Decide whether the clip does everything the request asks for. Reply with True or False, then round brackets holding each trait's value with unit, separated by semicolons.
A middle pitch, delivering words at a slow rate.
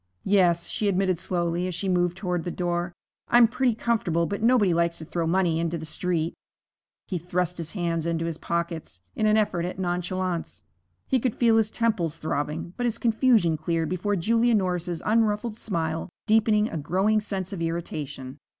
False (180 Hz; 175 wpm)